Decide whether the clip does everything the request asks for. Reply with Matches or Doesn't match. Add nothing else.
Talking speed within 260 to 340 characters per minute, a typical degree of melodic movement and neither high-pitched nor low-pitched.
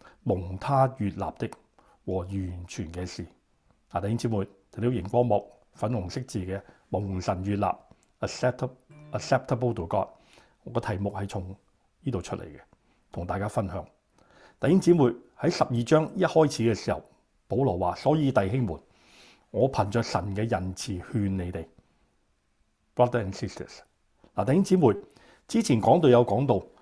Doesn't match